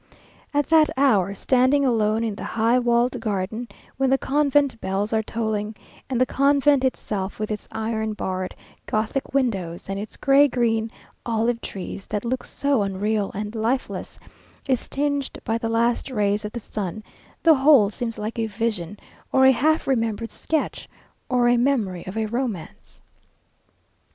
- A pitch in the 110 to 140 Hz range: No, high, 230 Hz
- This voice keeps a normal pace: Yes, average, 155 wpm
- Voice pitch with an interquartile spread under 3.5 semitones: No, average, 3.9 semitones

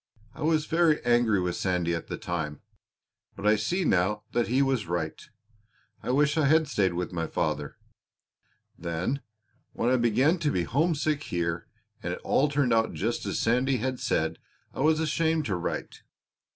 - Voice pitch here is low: Yes, low, 120 Hz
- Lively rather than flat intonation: Yes, wide, 8.9 semitones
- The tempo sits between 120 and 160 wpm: No, average, 175 wpm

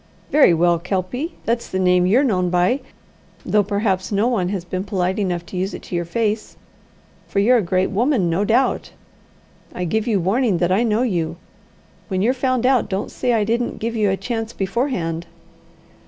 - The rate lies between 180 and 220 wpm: Yes, average, 190 wpm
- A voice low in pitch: No, high, 200 Hz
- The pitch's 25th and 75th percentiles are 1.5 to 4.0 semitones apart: No, average, 4.4 semitones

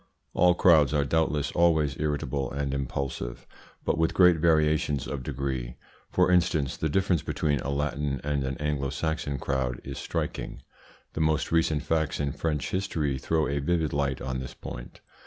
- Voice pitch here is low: Yes, very low, 75 Hz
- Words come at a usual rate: Yes, average, 165 wpm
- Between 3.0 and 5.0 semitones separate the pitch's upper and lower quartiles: No, narrow, 2.6 semitones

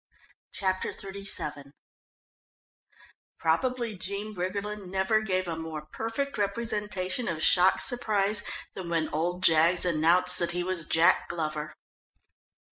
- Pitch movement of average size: Yes, average, 3.7 semitones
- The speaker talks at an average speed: No, slow, 115 wpm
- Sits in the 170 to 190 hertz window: Yes, medium, 185 Hz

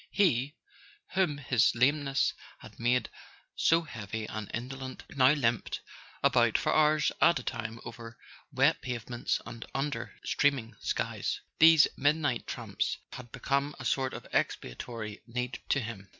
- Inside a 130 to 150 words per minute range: Yes, average, 140 wpm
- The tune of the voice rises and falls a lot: No, average, 3.6 semitones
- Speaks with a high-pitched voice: No, low, 130 Hz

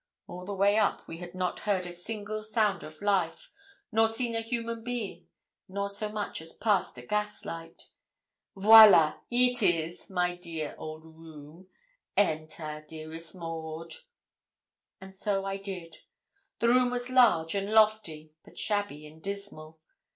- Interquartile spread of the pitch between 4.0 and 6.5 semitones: Yes, average, 4.7 semitones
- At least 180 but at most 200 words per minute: No, average, 145 wpm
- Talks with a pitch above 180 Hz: Yes, high, 190 Hz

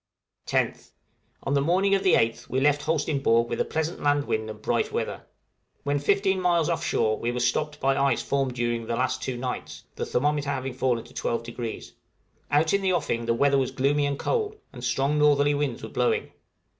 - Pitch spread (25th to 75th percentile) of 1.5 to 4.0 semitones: Yes, average, 3.5 semitones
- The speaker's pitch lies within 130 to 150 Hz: Yes, medium, 140 Hz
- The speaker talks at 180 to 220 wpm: Yes, average, 200 wpm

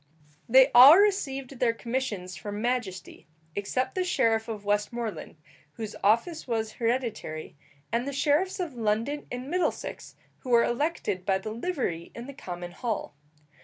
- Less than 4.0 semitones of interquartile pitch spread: No, average, 4.5 semitones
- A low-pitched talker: No, high, 235 Hz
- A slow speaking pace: No, average, 145 wpm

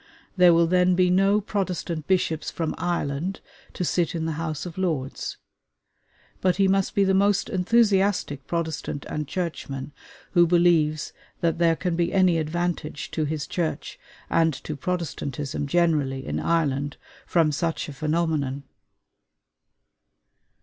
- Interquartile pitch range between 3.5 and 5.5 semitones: No, average, 3.0 semitones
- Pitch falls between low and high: Yes, medium, 170 Hz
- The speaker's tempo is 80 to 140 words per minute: Yes, slow, 135 wpm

